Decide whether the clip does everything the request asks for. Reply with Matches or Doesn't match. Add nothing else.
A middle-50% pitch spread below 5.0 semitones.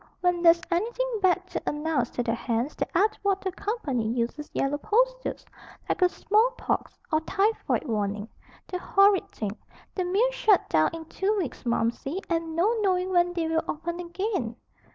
Doesn't match